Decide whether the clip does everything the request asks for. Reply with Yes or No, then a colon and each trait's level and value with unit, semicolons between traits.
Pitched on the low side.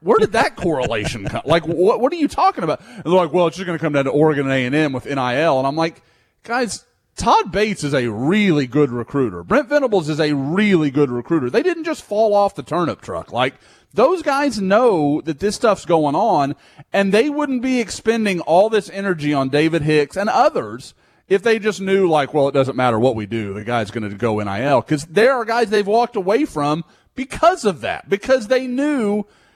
No: medium, 170 Hz